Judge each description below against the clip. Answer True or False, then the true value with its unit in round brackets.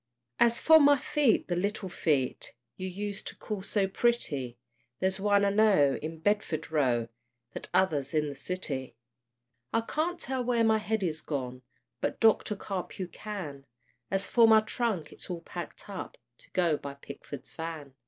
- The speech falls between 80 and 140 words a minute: False (165 wpm)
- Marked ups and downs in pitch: True (6.3 semitones)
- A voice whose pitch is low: False (190 Hz)